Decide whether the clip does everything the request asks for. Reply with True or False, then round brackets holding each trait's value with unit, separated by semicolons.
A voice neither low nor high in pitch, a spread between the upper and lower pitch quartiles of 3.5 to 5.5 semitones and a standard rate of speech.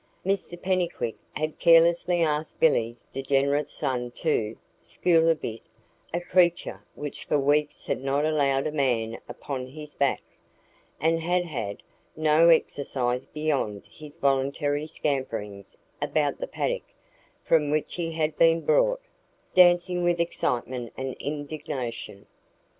False (150 Hz; 3.9 semitones; 125 wpm)